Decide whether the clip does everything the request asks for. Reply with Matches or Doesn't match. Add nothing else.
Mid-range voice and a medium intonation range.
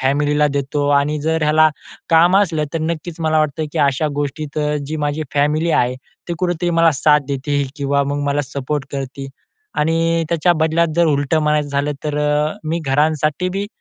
Doesn't match